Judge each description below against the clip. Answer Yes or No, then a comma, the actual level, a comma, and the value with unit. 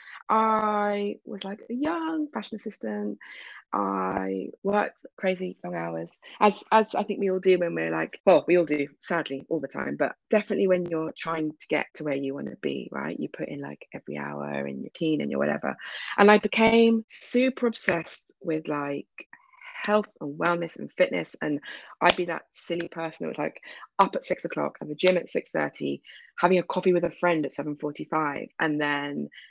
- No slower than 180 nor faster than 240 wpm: Yes, average, 200 wpm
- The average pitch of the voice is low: No, medium, 170 Hz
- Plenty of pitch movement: Yes, wide, 6.4 semitones